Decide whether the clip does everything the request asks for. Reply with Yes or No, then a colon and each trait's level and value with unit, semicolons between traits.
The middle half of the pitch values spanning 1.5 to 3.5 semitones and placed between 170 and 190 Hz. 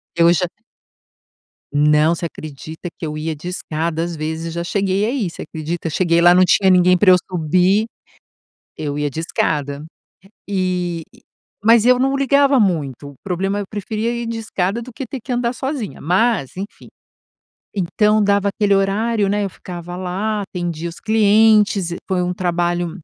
No: average, 4.0 semitones; medium, 185 Hz